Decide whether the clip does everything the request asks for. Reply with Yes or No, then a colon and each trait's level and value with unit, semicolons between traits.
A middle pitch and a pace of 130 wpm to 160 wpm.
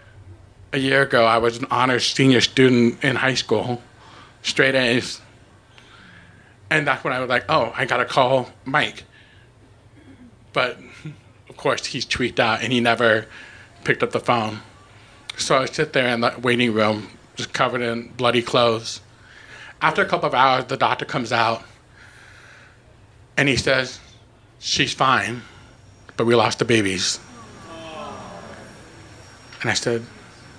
No: low, 120 Hz; average, 145 wpm